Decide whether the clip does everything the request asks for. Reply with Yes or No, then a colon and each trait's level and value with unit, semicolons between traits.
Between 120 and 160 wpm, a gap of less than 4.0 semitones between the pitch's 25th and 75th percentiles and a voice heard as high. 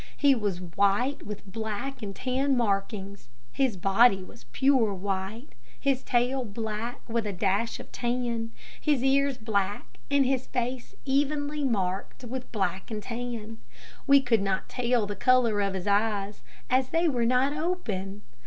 No: average, 155 wpm; average, 4.5 semitones; high, 230 Hz